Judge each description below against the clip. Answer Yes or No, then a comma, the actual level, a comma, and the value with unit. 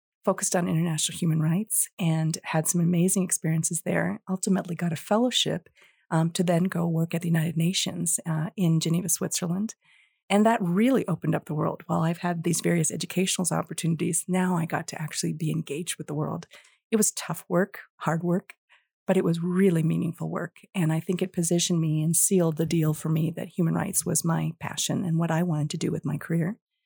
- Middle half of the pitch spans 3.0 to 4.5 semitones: No, narrow, 2.4 semitones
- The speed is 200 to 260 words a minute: Yes, fast, 205 wpm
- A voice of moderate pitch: Yes, medium, 170 Hz